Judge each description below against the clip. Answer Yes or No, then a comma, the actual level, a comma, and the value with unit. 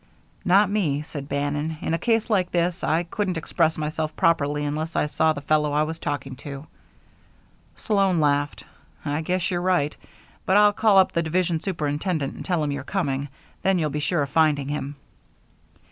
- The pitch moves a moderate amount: Yes, average, 3.7 semitones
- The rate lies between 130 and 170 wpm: No, average, 180 wpm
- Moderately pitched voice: Yes, medium, 155 Hz